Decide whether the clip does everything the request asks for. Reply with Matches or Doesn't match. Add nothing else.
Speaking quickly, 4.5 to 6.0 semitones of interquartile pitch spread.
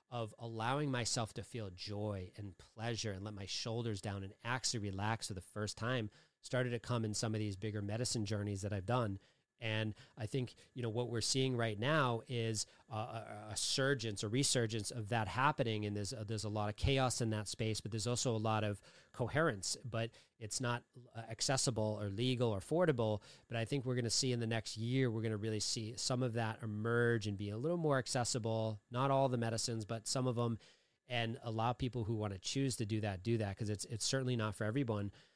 Doesn't match